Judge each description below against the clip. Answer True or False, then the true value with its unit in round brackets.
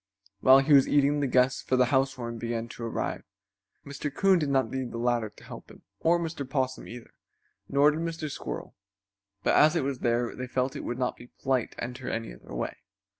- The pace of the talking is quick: True (215 wpm)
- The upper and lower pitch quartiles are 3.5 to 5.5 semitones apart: False (2.9 semitones)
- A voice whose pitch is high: False (130 Hz)